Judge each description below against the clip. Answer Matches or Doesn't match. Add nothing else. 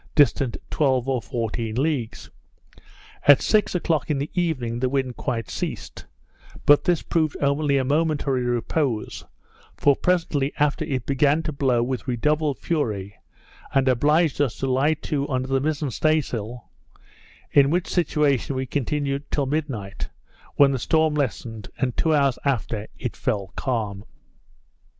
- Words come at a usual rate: Matches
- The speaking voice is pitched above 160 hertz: Doesn't match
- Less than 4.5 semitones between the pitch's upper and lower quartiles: Matches